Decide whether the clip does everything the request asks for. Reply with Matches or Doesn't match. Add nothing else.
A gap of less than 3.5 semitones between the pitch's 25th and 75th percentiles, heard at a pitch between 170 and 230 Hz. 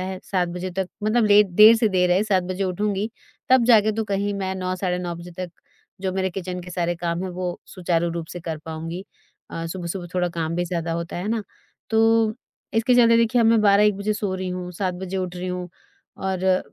Matches